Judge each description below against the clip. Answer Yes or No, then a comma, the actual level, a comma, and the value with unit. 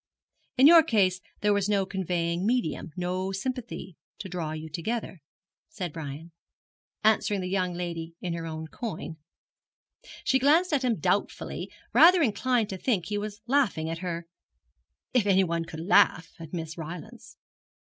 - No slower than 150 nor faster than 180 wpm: Yes, average, 155 wpm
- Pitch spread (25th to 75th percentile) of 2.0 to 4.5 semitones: No, average, 5.1 semitones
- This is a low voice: No, medium, 185 Hz